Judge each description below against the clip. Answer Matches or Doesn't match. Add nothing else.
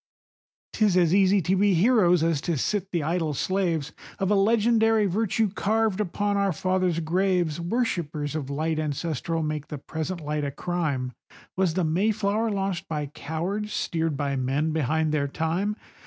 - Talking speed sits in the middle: Matches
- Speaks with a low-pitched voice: Doesn't match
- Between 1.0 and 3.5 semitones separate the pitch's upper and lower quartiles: Doesn't match